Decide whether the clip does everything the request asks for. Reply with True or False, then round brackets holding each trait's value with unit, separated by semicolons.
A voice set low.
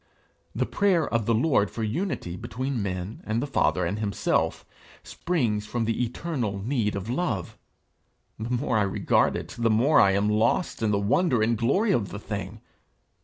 True (115 Hz)